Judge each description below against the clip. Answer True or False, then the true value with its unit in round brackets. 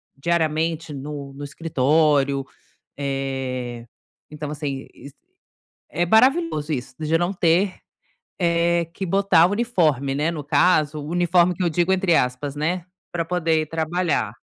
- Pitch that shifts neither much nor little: True (3.4 semitones)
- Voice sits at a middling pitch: True (160 Hz)